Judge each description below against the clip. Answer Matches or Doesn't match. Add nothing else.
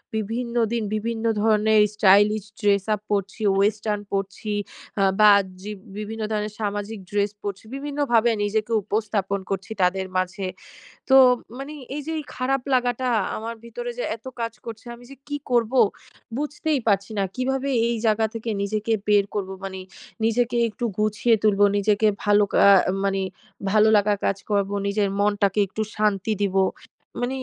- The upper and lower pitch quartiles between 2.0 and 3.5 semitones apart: Matches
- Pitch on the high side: Matches